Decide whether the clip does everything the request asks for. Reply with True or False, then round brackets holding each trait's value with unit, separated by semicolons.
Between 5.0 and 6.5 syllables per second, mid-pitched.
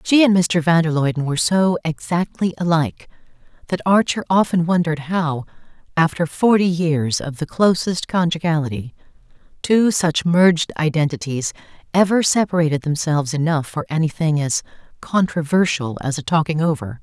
True (5.2 syllables/s; 165 Hz)